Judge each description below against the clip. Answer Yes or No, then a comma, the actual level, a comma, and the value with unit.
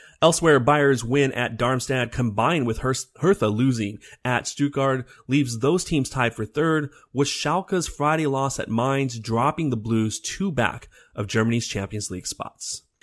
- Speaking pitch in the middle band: No, low, 130 Hz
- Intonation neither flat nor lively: Yes, average, 4.2 semitones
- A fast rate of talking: No, average, 155 wpm